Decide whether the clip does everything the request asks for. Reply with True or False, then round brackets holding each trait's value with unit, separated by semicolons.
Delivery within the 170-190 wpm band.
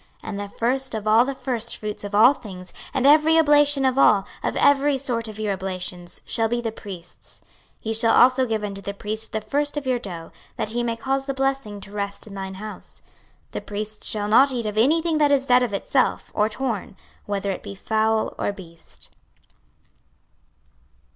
False (200 wpm)